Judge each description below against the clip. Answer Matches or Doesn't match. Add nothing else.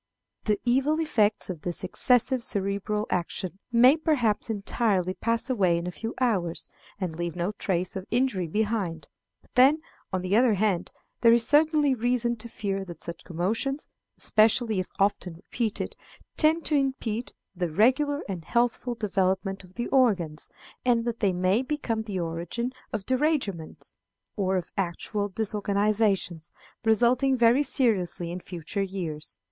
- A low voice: Doesn't match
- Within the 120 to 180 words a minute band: Matches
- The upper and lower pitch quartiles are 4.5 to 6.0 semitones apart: Matches